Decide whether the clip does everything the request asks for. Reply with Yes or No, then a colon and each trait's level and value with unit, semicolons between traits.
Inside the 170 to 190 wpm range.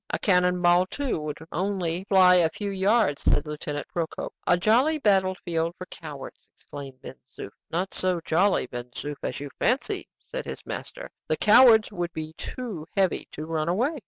Yes: average, 180 wpm